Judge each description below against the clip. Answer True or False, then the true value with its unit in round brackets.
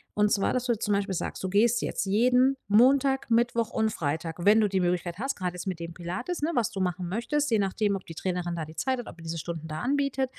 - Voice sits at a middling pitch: False (200 Hz)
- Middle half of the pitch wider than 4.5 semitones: True (5.5 semitones)